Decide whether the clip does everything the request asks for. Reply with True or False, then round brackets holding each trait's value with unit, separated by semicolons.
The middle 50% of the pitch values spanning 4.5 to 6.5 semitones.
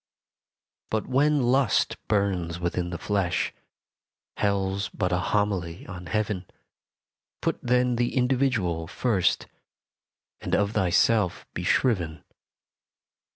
True (5.2 semitones)